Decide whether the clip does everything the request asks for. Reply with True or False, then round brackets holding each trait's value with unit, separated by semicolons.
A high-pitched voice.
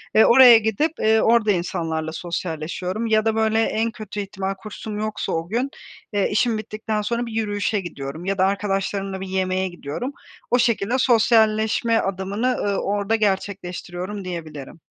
True (205 Hz)